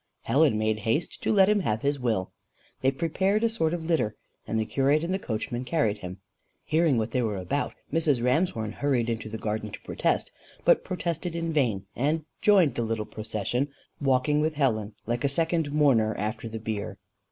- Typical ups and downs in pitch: No, wide, 6.5 semitones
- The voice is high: No, low, 130 Hz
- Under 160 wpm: No, average, 190 wpm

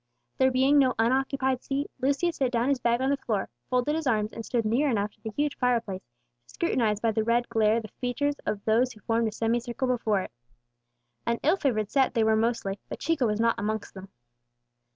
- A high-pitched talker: Yes, high, 235 Hz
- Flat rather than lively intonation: No, average, 3.3 semitones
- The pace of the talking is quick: Yes, fast, 215 wpm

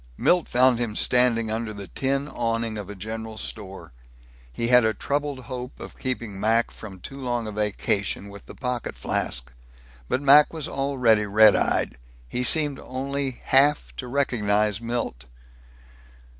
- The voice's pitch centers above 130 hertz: No, low, 115 Hz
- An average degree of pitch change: Yes, average, 3.8 semitones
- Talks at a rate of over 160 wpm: No, average, 155 wpm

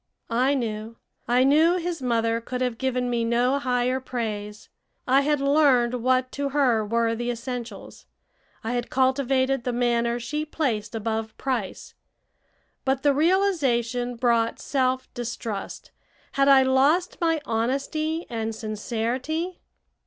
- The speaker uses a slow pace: Yes, slow, 130 wpm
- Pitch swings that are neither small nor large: Yes, average, 3.0 semitones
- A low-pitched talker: No, very high, 250 Hz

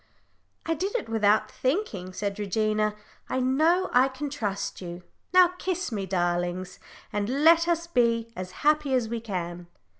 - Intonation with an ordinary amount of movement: No, wide, 7.4 semitones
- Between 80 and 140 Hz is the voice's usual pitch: No, high, 230 Hz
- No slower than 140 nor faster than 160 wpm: Yes, average, 155 wpm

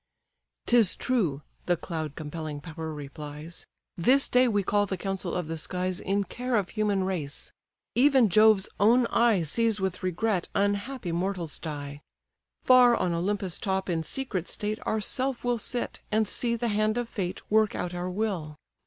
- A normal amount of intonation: Yes, average, 4.7 semitones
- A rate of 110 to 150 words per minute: No, average, 160 wpm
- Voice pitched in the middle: No, high, 195 Hz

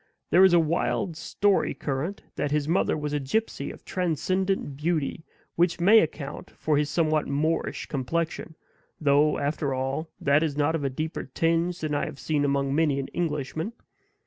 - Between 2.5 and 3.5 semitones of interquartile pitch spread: Yes, average, 2.8 semitones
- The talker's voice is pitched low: No, medium, 155 Hz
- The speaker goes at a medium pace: Yes, average, 170 wpm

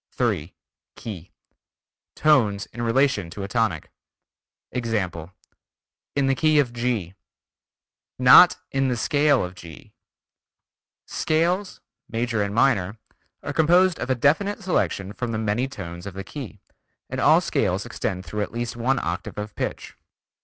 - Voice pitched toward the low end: Yes, low, 115 Hz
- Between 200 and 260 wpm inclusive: No, average, 140 wpm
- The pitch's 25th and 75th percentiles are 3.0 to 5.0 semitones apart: No, wide, 5.5 semitones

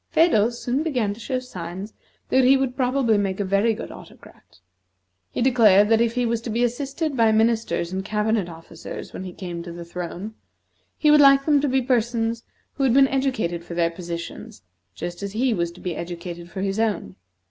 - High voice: Yes, high, 220 Hz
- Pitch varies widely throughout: Yes, wide, 6.0 semitones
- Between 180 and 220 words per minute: Yes, average, 200 wpm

